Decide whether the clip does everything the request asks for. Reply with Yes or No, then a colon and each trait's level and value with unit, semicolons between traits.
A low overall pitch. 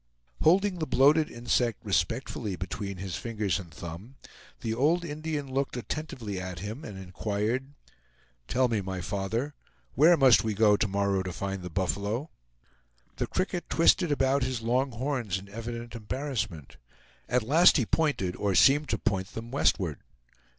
Yes: low, 115 Hz